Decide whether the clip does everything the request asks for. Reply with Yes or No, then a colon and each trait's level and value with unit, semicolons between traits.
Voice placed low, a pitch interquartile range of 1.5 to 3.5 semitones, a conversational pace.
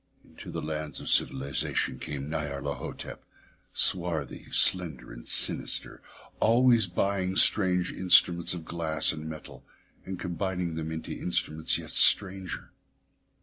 No: very low, 85 Hz; average, 3.2 semitones; slow, 115 wpm